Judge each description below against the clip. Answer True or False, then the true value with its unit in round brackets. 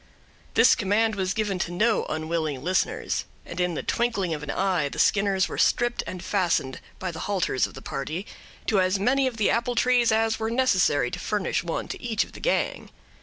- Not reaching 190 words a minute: False (205 wpm)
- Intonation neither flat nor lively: True (4.7 semitones)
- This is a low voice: False (195 Hz)